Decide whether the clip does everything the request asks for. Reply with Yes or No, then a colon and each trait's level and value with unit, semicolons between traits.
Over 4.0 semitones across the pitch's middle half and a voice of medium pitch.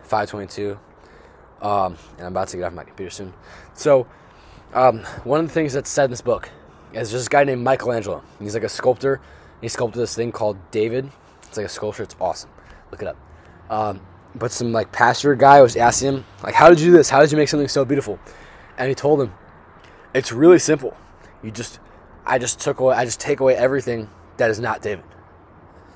No: average, 4.9 semitones; low, 120 Hz